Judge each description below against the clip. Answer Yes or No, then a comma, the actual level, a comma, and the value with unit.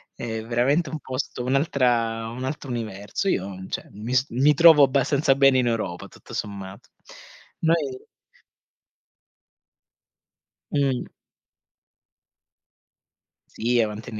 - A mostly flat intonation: No, average, 3.6 semitones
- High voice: No, low, 125 Hz